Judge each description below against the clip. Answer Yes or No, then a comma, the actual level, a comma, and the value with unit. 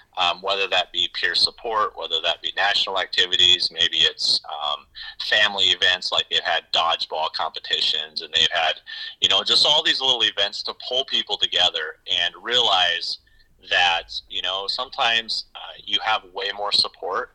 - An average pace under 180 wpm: Yes, average, 165 wpm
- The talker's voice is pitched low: No, very high, 385 Hz